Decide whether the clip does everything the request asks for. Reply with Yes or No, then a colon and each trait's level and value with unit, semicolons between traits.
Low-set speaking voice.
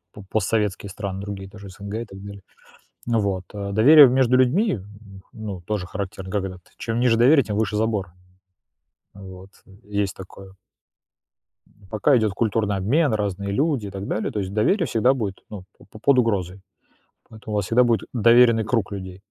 Yes: low, 105 Hz